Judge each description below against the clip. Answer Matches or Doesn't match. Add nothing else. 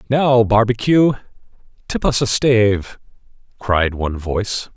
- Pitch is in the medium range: Doesn't match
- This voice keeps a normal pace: Doesn't match